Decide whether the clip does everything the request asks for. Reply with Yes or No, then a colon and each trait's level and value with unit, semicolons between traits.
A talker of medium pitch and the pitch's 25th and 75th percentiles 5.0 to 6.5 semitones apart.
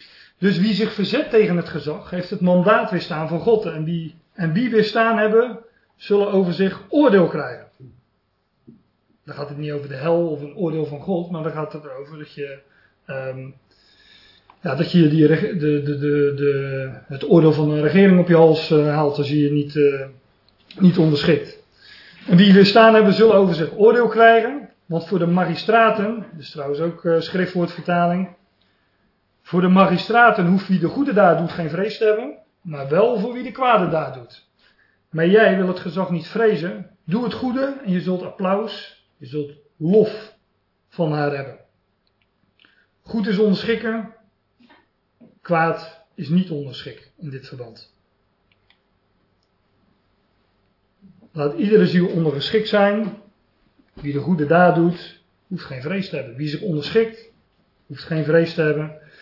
Yes: medium, 170 Hz; wide, 5.6 semitones